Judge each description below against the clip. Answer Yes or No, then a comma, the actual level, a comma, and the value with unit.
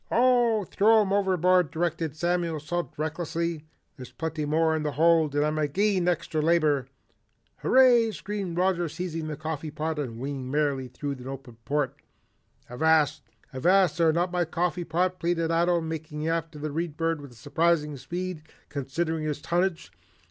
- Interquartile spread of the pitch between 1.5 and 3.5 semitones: Yes, average, 2.8 semitones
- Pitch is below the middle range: No, medium, 160 Hz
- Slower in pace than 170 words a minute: Yes, average, 160 wpm